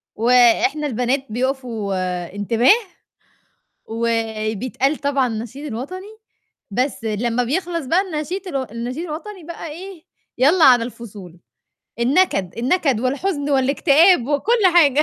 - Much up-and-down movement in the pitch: Yes, wide, 5.8 semitones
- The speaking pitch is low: No, very high, 265 Hz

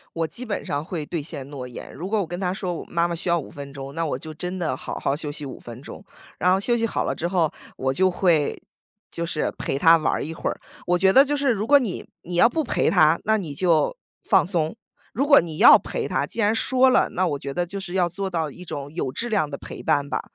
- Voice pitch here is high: No, medium, 175 Hz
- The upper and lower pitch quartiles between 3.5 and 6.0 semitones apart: Yes, average, 4.7 semitones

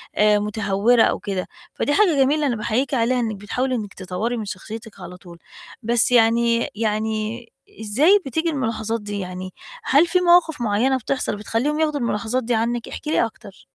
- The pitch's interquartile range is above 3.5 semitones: Yes, average, 3.9 semitones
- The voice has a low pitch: No, high, 230 Hz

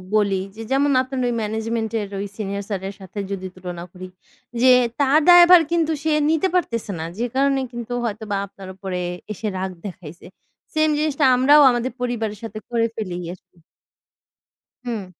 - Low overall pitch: No, high, 225 Hz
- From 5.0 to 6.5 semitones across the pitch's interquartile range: Yes, wide, 5.4 semitones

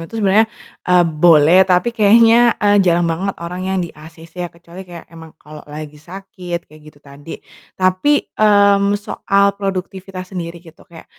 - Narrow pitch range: No, average, 3.3 semitones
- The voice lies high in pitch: No, medium, 180 Hz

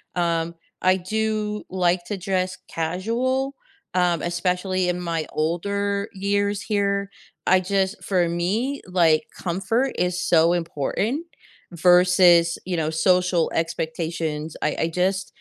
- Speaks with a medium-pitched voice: Yes, medium, 180 Hz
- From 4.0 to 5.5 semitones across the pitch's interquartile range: No, average, 2.8 semitones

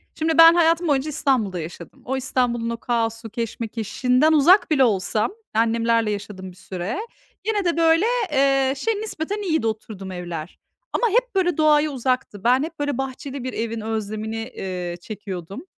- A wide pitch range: Yes, wide, 6.4 semitones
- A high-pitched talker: Yes, very high, 250 Hz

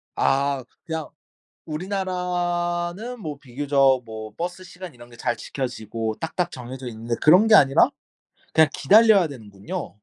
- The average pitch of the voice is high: No, medium, 145 Hz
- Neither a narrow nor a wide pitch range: No, wide, 6.6 semitones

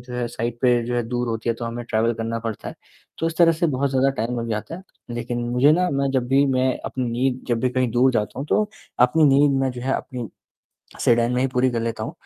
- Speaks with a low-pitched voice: Yes, low, 125 Hz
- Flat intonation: Yes, narrow, 2.3 semitones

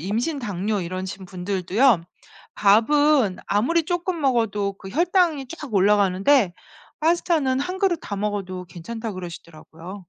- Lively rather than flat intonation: Yes, wide, 7.5 semitones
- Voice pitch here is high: Yes, high, 210 Hz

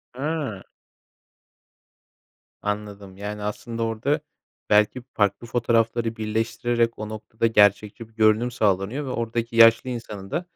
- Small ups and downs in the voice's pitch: Yes, narrow, 2.1 semitones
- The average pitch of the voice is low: Yes, low, 115 Hz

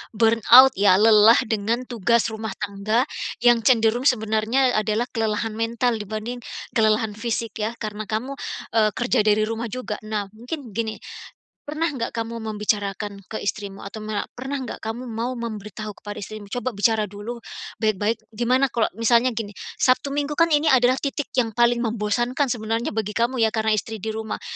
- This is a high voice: Yes, high, 225 Hz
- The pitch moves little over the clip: Yes, narrow, 2.2 semitones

